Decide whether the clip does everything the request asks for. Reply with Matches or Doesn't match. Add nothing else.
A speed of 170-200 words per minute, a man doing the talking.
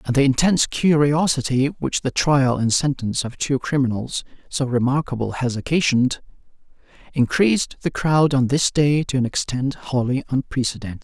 Doesn't match